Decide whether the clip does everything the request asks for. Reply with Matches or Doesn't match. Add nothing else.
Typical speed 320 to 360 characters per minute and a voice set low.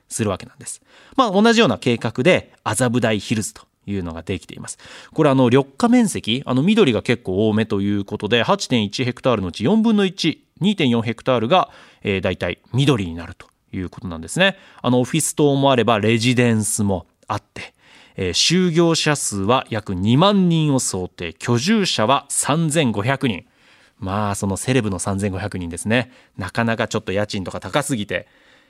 Matches